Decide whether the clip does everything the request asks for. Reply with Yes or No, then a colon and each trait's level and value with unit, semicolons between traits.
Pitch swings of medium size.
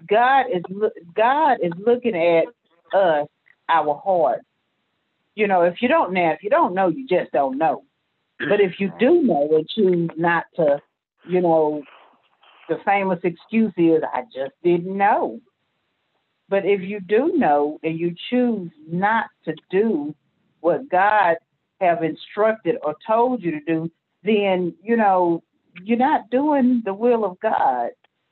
Yes: average, 4.7 semitones